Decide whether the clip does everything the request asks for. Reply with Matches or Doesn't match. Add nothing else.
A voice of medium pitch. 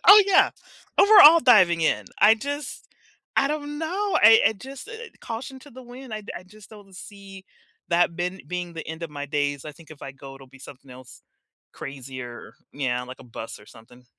Matches